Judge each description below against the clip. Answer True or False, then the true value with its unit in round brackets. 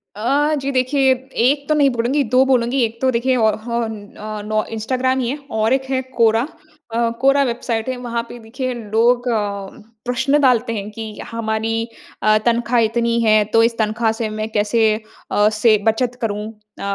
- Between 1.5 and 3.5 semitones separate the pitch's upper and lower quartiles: True (2.8 semitones)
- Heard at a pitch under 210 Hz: False (235 Hz)